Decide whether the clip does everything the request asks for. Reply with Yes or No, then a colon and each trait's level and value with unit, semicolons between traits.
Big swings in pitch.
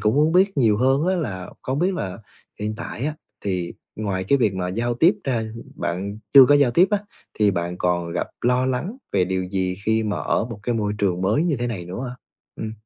Yes: wide, 6.2 semitones